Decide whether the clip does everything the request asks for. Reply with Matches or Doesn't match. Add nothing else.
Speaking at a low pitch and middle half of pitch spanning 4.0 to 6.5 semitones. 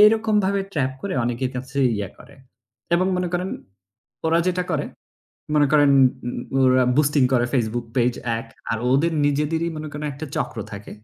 Doesn't match